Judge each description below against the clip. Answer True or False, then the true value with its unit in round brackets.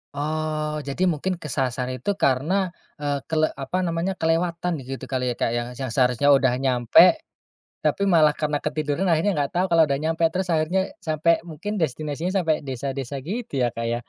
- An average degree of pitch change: True (3.7 semitones)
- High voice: False (155 Hz)